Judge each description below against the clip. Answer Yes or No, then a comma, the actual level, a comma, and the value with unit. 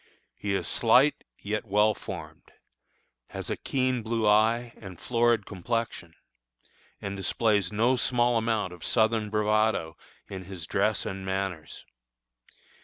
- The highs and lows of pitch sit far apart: No, average, 3.1 semitones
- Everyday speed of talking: No, slow, 125 wpm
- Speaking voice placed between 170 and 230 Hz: No, low, 105 Hz